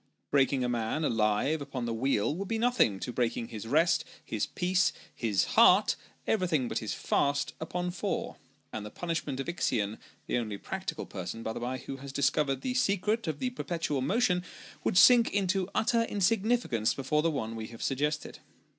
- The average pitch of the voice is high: No, medium, 140 Hz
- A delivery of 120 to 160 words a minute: No, average, 180 wpm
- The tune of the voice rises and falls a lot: Yes, wide, 7.5 semitones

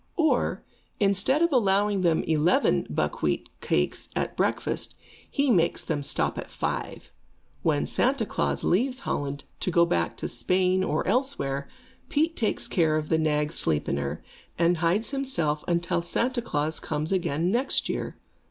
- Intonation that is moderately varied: No, wide, 7.4 semitones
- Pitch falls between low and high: Yes, medium, 175 Hz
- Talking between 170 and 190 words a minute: No, average, 145 wpm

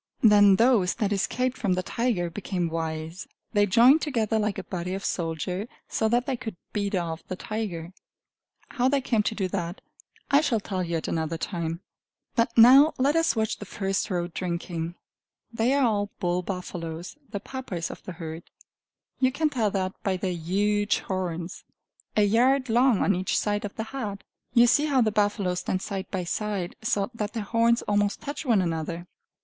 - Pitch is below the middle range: No, high, 205 Hz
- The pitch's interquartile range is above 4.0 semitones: Yes, average, 4.4 semitones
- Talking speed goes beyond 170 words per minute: Yes, average, 185 wpm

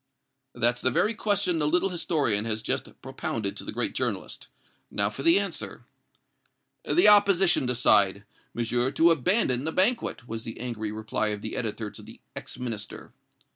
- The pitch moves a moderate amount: No, wide, 8.4 semitones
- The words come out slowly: No, average, 165 wpm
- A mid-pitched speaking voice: No, low, 125 Hz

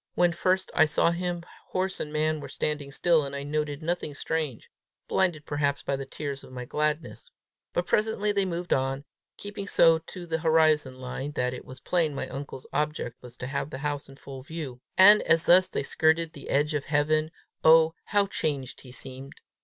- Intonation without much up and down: No, average, 3.4 semitones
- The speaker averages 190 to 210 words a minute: Yes, average, 195 wpm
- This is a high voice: No, medium, 150 Hz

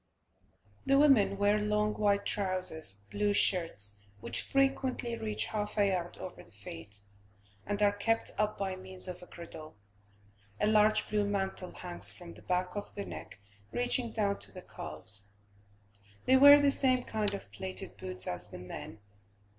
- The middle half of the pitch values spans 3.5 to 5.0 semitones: Yes, average, 3.9 semitones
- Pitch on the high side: Yes, high, 200 Hz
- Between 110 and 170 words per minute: Yes, average, 160 wpm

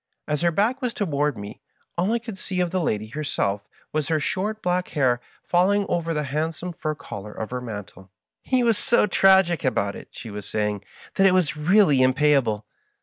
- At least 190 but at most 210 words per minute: Yes, fast, 205 wpm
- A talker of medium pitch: Yes, medium, 155 Hz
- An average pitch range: No, wide, 7.3 semitones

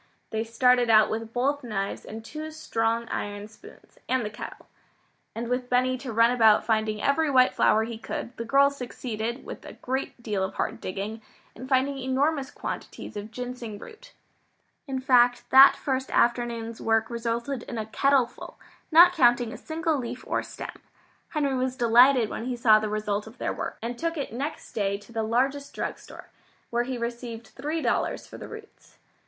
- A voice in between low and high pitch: No, high, 240 Hz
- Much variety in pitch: No, average, 3.1 semitones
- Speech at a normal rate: Yes, average, 185 wpm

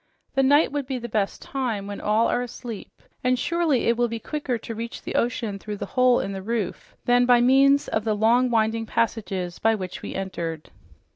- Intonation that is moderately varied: Yes, average, 3.2 semitones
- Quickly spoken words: Yes, fast, 210 wpm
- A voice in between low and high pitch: No, high, 230 Hz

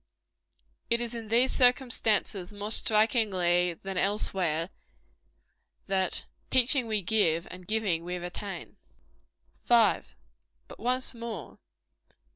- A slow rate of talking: Yes, slow, 105 wpm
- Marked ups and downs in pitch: No, average, 4.5 semitones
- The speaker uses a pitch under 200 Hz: No, high, 210 Hz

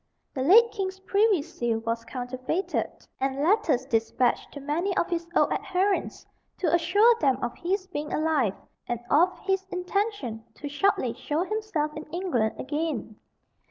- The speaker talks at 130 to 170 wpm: Yes, average, 150 wpm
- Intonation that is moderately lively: No, wide, 6.6 semitones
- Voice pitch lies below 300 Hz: No, very high, 320 Hz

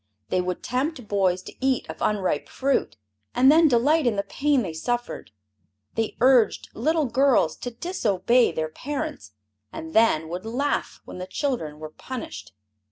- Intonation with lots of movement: Yes, wide, 6.9 semitones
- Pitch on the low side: No, high, 235 Hz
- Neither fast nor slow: Yes, average, 160 wpm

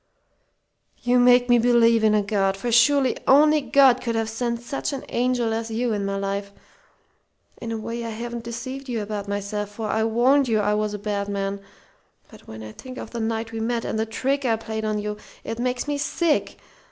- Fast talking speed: Yes, fast, 215 wpm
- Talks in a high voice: Yes, high, 230 Hz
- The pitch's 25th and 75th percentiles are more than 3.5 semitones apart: No, average, 2.7 semitones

